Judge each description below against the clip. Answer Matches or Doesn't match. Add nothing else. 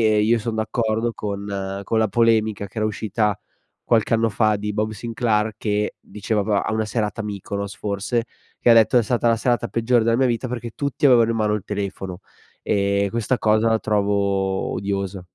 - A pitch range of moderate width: Doesn't match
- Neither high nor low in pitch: Doesn't match